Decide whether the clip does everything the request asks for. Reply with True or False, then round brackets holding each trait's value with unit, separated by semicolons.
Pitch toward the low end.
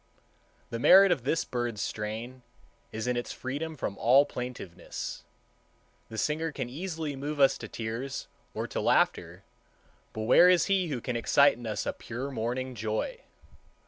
True (125 Hz)